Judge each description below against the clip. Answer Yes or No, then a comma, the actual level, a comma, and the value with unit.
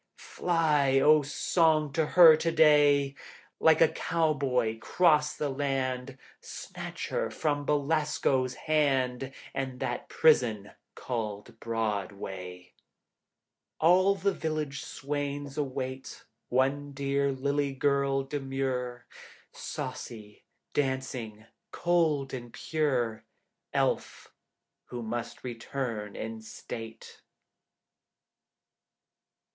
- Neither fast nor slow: No, slow, 90 wpm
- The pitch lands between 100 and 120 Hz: No, low, 135 Hz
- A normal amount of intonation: Yes, average, 3.5 semitones